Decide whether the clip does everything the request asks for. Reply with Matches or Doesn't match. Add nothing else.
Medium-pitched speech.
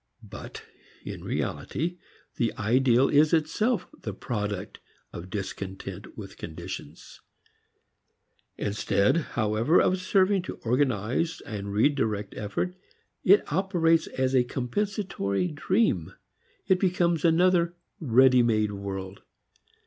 Doesn't match